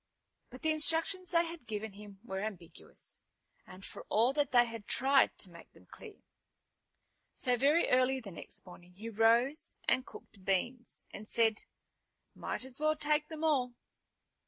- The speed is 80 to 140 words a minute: No, average, 160 wpm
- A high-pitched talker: Yes, high, 245 Hz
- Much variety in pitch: Yes, wide, 6.0 semitones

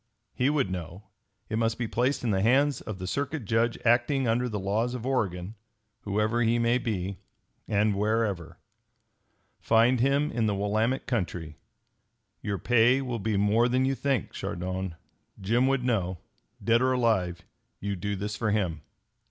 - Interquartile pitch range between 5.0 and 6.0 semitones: No, average, 3.9 semitones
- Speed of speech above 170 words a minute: No, average, 160 wpm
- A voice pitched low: Yes, low, 110 Hz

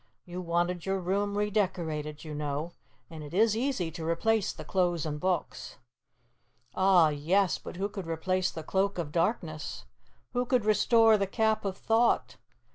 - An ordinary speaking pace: Yes, average, 165 wpm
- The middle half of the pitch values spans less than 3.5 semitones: No, average, 4.0 semitones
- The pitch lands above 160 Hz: Yes, medium, 185 Hz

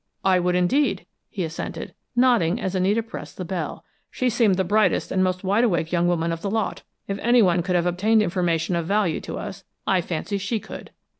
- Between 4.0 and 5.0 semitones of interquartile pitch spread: No, average, 3.4 semitones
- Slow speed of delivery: No, fast, 205 wpm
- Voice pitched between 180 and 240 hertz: Yes, medium, 185 Hz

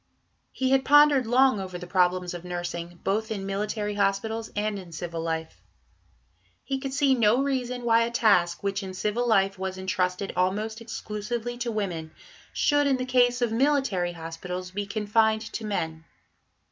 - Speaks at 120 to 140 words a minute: No, average, 165 wpm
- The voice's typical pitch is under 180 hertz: No, high, 210 Hz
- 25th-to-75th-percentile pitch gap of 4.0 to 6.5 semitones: Yes, average, 4.8 semitones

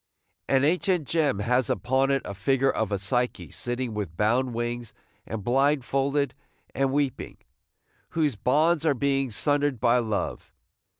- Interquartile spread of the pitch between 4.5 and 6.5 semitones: No, average, 3.1 semitones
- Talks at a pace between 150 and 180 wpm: No, average, 140 wpm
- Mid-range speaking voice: No, low, 130 Hz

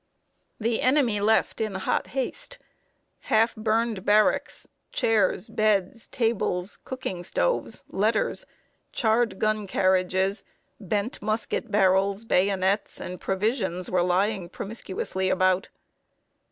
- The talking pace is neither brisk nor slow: No, slow, 100 wpm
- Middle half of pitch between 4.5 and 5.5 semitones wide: No, average, 3.0 semitones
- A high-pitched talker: Yes, high, 205 Hz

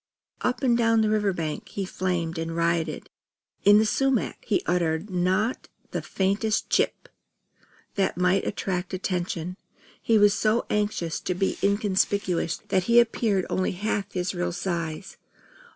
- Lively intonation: No, average, 3.0 semitones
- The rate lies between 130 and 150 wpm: Yes, average, 145 wpm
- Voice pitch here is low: No, high, 190 Hz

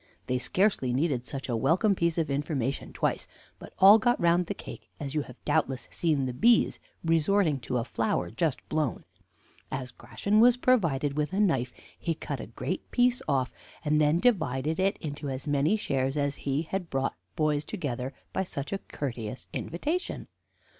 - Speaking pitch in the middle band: Yes, medium, 150 Hz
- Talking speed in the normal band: Yes, average, 175 wpm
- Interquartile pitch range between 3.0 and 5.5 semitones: Yes, average, 5.1 semitones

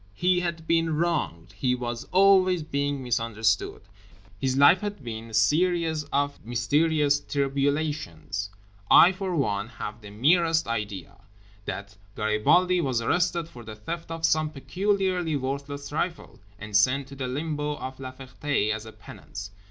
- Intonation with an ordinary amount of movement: No, wide, 6.3 semitones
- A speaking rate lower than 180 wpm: Yes, average, 145 wpm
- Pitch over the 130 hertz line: Yes, medium, 140 Hz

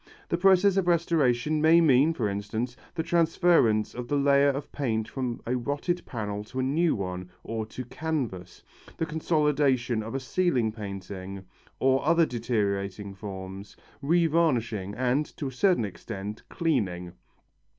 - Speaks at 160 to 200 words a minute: No, average, 145 wpm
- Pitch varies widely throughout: Yes, wide, 7.0 semitones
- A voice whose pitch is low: Yes, low, 125 Hz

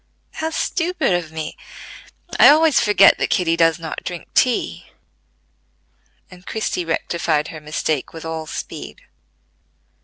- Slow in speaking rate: Yes, slow, 125 wpm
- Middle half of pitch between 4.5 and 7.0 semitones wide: Yes, average, 5.3 semitones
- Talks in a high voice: No, medium, 170 Hz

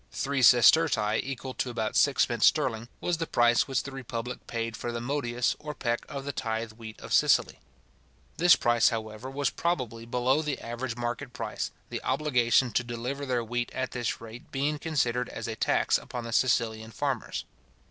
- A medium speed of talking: Yes, average, 180 wpm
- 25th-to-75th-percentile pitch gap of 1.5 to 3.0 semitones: Yes, average, 2.7 semitones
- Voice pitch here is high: No, low, 120 Hz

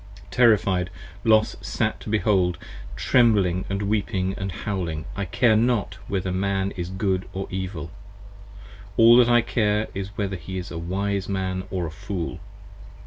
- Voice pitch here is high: No, very low, 95 Hz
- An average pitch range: No, narrow, 2.3 semitones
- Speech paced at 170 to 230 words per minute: No, average, 160 wpm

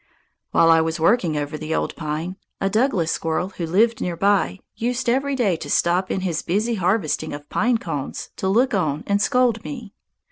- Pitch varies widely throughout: Yes, wide, 5.9 semitones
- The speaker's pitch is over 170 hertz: Yes, high, 190 Hz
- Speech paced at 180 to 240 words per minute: Yes, average, 190 wpm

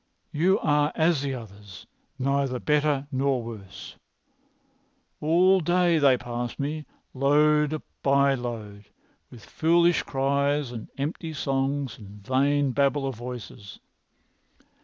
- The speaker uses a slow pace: Yes, slow, 115 wpm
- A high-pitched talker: No, medium, 140 Hz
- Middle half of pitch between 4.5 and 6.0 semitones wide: No, average, 3.5 semitones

